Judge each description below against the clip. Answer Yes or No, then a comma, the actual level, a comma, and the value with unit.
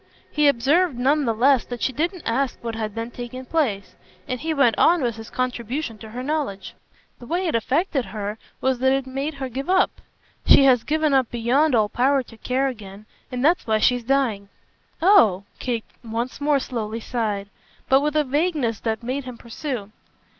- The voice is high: Yes, very high, 255 Hz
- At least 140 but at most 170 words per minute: No, average, 190 wpm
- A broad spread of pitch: No, average, 3.8 semitones